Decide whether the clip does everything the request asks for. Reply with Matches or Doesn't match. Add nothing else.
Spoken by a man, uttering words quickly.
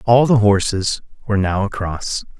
Doesn't match